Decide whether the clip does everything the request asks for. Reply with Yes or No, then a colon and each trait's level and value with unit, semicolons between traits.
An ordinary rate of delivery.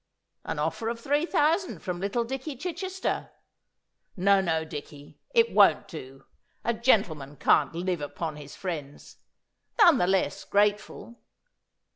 No: slow, 130 wpm